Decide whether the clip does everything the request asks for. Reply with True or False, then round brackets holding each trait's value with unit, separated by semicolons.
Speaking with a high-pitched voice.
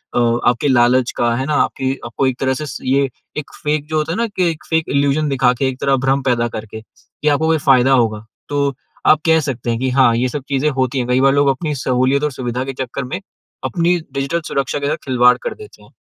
False (135 Hz)